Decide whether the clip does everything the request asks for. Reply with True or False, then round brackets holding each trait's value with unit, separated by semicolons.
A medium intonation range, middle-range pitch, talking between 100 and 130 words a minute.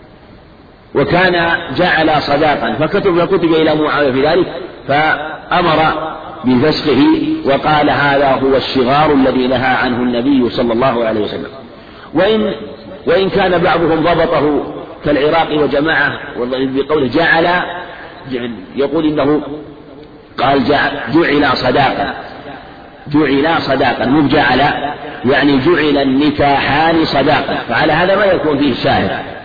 True (3.3 semitones; 145 Hz; 105 wpm)